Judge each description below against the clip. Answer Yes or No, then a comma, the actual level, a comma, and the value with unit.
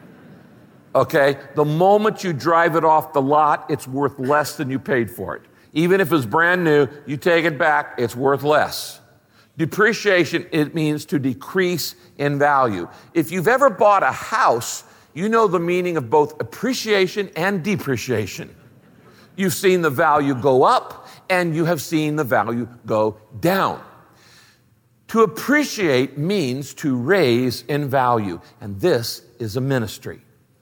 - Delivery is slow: No, average, 150 wpm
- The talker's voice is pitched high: No, medium, 150 Hz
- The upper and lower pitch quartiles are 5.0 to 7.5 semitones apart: Yes, wide, 5.5 semitones